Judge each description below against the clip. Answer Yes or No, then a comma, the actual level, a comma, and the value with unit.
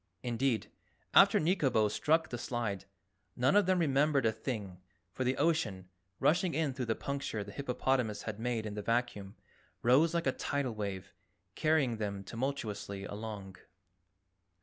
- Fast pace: No, average, 150 wpm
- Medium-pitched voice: No, low, 120 Hz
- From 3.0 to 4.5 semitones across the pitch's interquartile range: No, average, 5.1 semitones